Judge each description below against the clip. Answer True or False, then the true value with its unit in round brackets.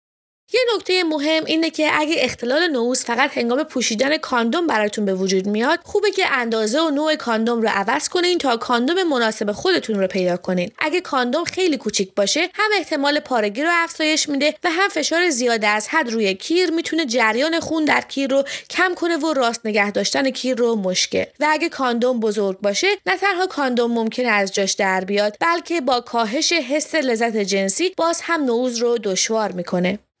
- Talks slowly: False (180 wpm)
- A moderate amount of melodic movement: False (6.7 semitones)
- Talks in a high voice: True (265 Hz)